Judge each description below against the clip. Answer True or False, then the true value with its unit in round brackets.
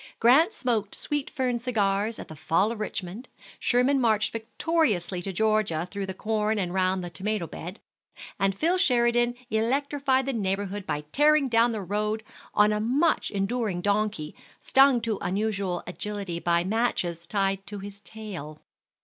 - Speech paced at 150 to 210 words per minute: True (155 wpm)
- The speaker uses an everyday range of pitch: True (3.9 semitones)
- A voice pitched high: True (210 Hz)